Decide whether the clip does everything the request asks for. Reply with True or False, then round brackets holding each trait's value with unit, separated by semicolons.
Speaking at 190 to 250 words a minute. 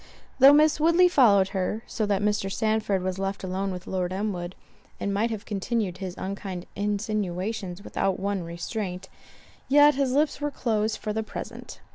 False (165 wpm)